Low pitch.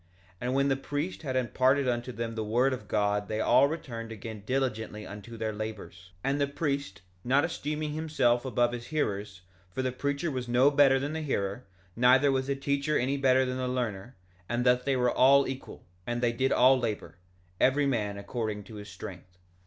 Yes: low, 125 Hz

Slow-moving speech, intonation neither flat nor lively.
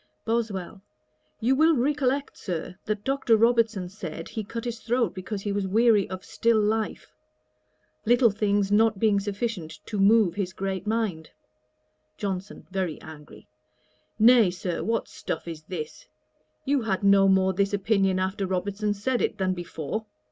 No: average, 150 wpm; average, 3.2 semitones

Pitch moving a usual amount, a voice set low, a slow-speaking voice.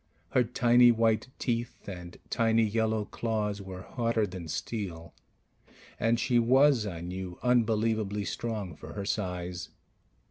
Yes: average, 3.6 semitones; low, 110 Hz; slow, 130 wpm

